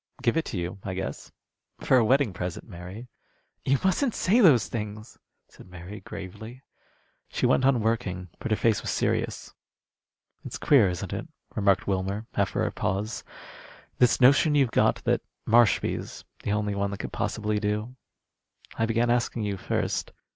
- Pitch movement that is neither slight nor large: Yes, average, 3.8 semitones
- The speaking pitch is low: Yes, low, 110 Hz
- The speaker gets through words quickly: No, average, 160 wpm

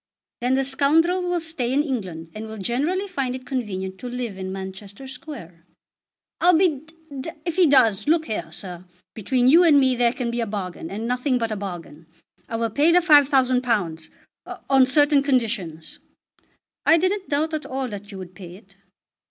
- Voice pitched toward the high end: Yes, very high, 250 Hz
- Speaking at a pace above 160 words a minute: Yes, average, 185 wpm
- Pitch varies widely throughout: Yes, wide, 6.8 semitones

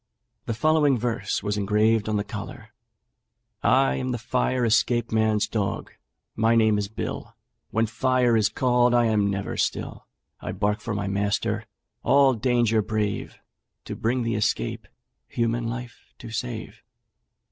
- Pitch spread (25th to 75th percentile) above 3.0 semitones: No, narrow, 2.6 semitones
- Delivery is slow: No, average, 145 wpm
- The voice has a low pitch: Yes, low, 115 Hz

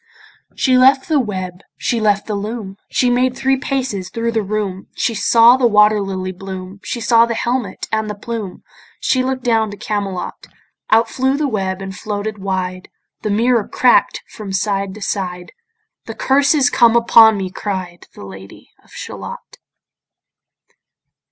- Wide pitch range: No, average, 3.8 semitones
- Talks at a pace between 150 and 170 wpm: Yes, average, 165 wpm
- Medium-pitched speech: No, high, 215 Hz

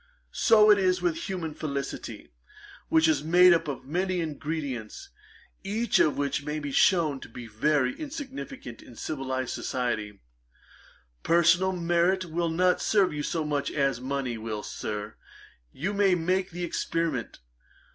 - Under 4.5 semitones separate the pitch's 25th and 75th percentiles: No, average, 5.0 semitones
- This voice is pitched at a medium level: Yes, medium, 160 Hz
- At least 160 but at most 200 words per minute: No, average, 145 wpm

